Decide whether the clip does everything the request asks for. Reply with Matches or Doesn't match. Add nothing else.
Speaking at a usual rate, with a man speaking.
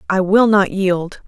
Doesn't match